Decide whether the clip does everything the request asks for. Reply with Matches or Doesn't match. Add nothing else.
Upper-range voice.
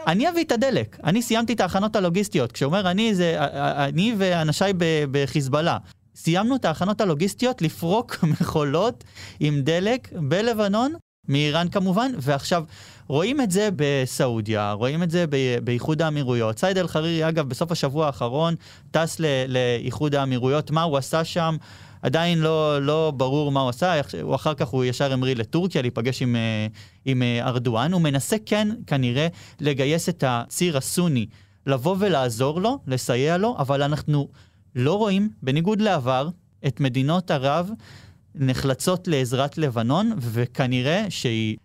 Doesn't match